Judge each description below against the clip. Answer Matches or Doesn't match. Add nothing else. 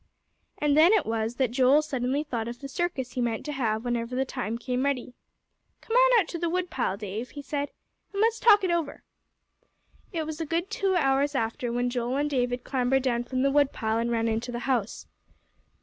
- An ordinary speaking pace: Doesn't match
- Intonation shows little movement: Doesn't match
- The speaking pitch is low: Doesn't match